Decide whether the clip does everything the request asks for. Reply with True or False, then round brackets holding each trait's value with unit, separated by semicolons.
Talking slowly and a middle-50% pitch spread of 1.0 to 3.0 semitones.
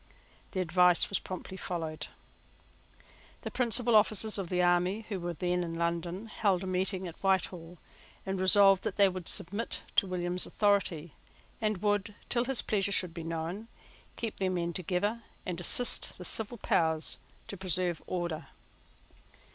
False (155 wpm; 2.6 semitones)